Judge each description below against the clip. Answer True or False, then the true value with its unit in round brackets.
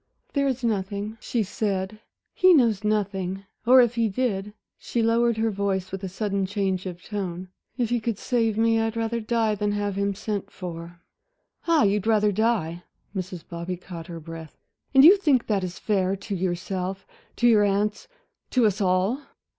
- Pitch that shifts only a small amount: False (3.2 semitones)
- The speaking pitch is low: False (205 Hz)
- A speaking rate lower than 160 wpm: False (180 wpm)